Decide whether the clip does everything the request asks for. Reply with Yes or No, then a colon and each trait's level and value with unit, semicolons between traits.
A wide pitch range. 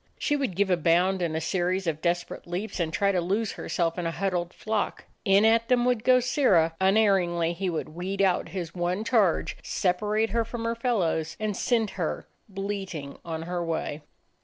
No: average, 4.0 semitones